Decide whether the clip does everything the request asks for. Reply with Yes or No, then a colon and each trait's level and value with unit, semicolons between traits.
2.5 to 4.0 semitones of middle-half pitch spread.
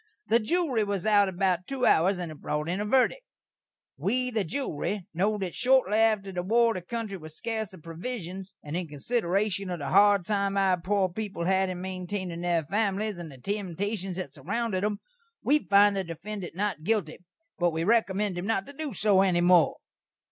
Yes: average, 3.4 semitones